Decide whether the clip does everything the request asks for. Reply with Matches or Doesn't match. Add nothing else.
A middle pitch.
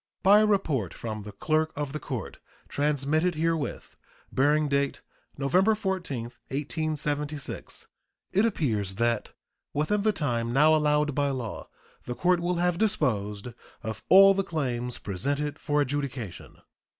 Matches